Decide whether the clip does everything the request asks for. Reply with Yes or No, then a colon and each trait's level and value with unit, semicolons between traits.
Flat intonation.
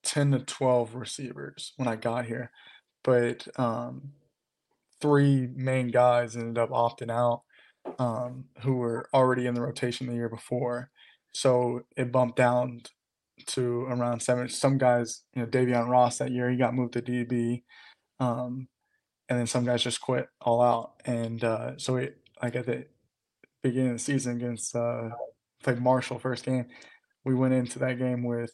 Yes: narrow, 1.2 semitones